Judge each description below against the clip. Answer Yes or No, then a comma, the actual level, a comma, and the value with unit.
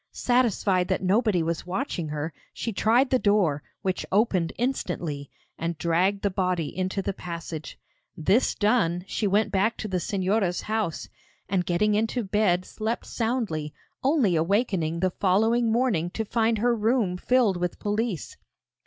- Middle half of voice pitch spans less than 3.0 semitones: No, average, 4.2 semitones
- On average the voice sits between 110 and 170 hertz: No, high, 195 Hz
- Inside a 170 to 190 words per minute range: No, average, 150 wpm